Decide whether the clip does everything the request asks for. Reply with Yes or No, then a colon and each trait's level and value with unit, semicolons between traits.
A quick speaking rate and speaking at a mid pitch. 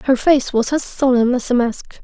No: fast, 235 wpm; very high, 255 Hz